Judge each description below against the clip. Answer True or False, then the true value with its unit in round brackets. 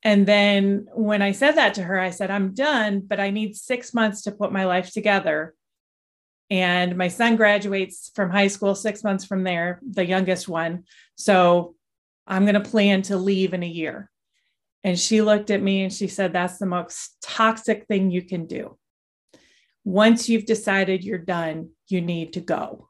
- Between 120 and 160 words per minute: False (185 wpm)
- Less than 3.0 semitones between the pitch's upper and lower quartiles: True (2.6 semitones)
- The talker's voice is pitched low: False (195 Hz)